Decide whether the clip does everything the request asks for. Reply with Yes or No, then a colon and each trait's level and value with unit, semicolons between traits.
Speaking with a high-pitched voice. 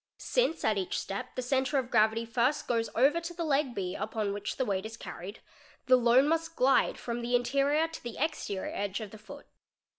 Yes: high, 245 Hz